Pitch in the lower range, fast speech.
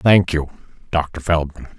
No: very low, 80 Hz; slow, 135 wpm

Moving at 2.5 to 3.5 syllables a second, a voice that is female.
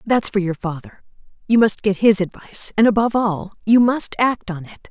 No: 5.4 syllables/s; female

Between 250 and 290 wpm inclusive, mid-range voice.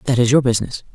No: fast, 255 wpm; low, 120 Hz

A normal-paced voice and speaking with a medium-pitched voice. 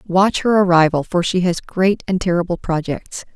Yes: average, 180 wpm; medium, 180 Hz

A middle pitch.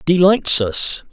Yes: medium, 160 Hz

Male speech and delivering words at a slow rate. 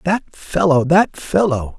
Yes: male; slow, 100 wpm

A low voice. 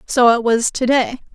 No: high, 245 Hz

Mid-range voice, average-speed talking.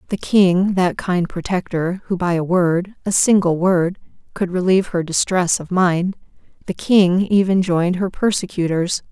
Yes: medium, 180 Hz; average, 160 wpm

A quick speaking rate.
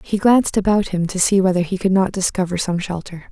Yes: fast, 235 wpm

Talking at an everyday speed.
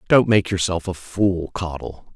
Yes: average, 165 wpm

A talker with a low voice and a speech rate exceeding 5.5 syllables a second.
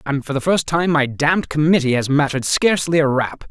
No: medium, 150 Hz; 6.0 syllables/s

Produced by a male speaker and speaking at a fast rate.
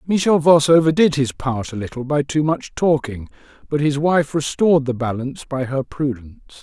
No: male; average, 180 wpm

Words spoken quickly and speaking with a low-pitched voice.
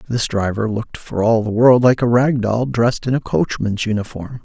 Yes: fast, 215 wpm; low, 115 Hz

